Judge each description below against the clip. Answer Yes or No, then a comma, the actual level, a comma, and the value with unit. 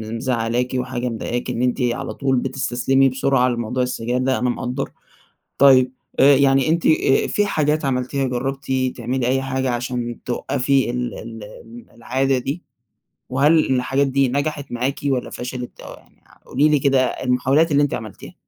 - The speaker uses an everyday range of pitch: No, narrow, 1.8 semitones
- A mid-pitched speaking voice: No, low, 130 Hz